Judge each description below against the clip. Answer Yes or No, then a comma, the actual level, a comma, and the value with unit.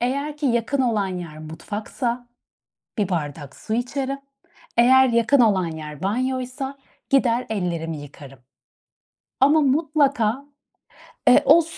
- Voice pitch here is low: No, high, 235 Hz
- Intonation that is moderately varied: No, wide, 7.1 semitones